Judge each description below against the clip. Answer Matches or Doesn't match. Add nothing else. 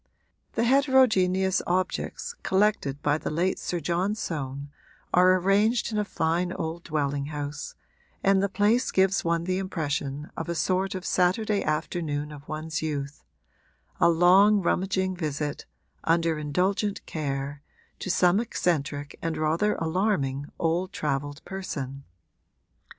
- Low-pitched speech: Doesn't match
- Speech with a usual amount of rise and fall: Matches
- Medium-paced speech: Doesn't match